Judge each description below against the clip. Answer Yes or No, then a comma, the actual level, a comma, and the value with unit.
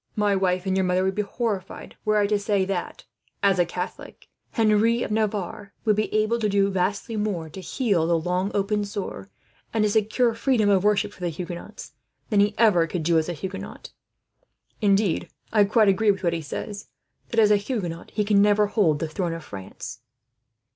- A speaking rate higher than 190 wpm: Yes, average, 200 wpm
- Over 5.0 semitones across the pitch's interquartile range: No, average, 2.8 semitones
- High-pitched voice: Yes, high, 200 Hz